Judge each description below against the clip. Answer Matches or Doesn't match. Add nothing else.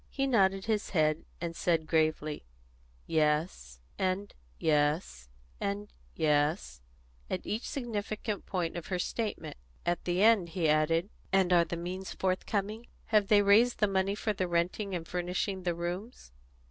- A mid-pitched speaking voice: Matches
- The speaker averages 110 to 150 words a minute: Matches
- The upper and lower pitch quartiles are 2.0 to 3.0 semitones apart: Doesn't match